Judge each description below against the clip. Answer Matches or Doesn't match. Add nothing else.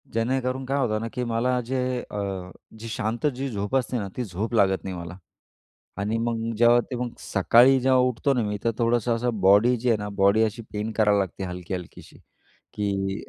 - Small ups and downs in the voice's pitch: Doesn't match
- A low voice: Matches